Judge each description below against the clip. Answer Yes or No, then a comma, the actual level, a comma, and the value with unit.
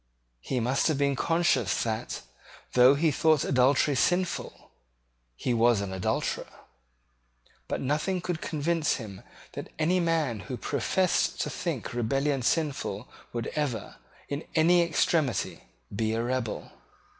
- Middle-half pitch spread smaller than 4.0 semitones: No, average, 5.2 semitones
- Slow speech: Yes, slow, 130 wpm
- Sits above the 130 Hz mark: Yes, medium, 140 Hz